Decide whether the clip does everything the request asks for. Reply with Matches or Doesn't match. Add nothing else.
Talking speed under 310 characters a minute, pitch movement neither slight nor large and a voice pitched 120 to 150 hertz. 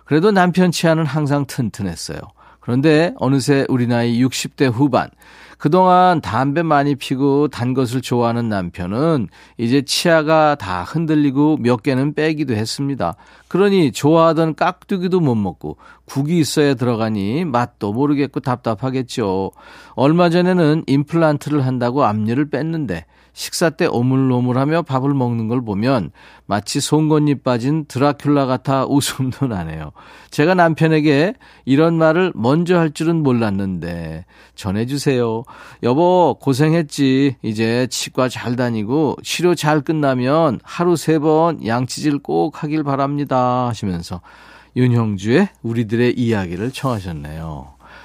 Matches